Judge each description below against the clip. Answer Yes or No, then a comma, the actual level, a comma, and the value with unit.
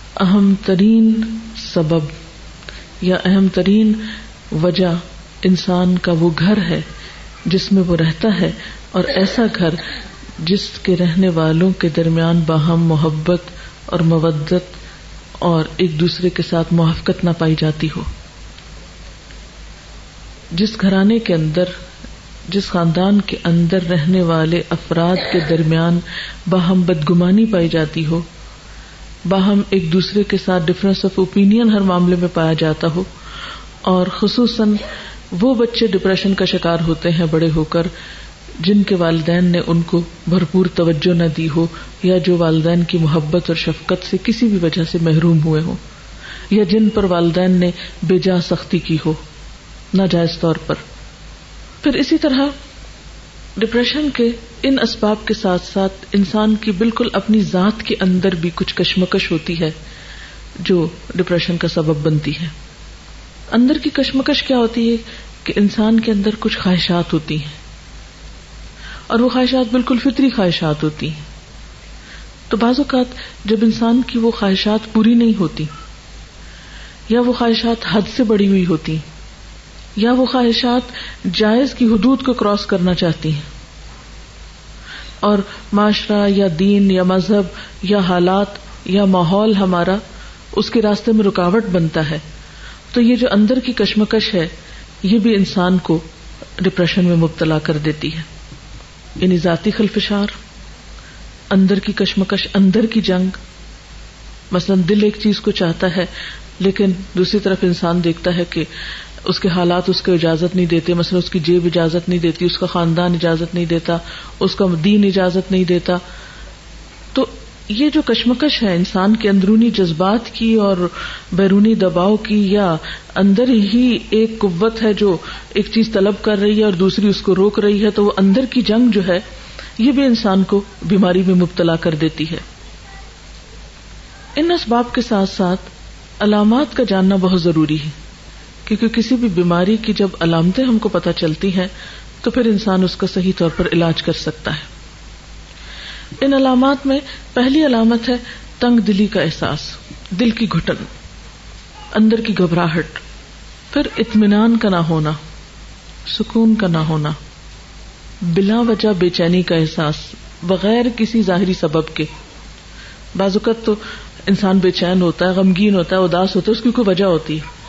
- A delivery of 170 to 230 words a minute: No, average, 155 wpm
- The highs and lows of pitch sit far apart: No, average, 3.9 semitones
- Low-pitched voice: No, medium, 185 Hz